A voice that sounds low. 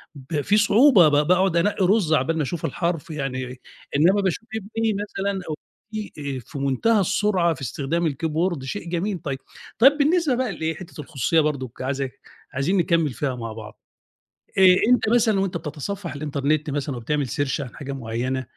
No: medium, 165 Hz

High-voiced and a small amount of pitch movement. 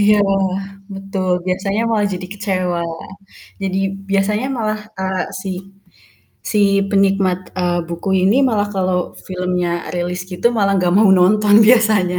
Yes: high, 195 Hz; narrow, 2.2 semitones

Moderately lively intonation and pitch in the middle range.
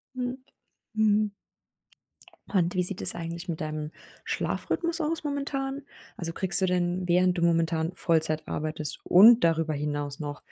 Yes: average, 4.9 semitones; medium, 175 Hz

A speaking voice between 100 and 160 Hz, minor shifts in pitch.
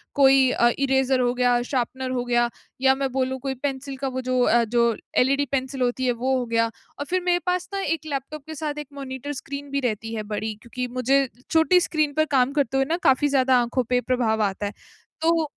No: very high, 265 Hz; narrow, 2.3 semitones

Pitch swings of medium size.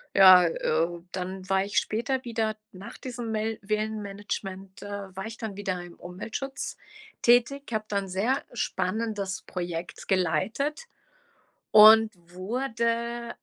Yes: average, 3.5 semitones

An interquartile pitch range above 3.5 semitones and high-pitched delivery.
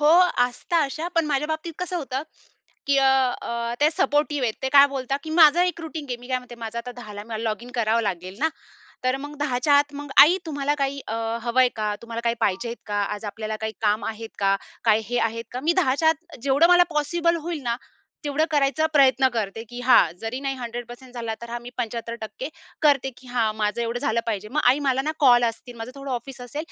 Yes: average, 4.1 semitones; very high, 255 Hz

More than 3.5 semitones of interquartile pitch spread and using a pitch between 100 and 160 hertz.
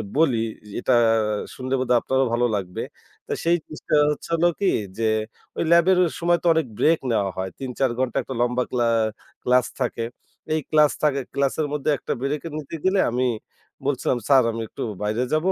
Yes: average, 4.0 semitones; low, 135 Hz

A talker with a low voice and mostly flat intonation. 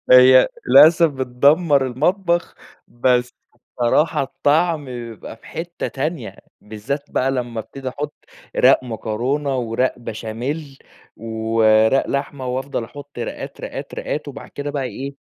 No: low, 130 Hz; average, 3.2 semitones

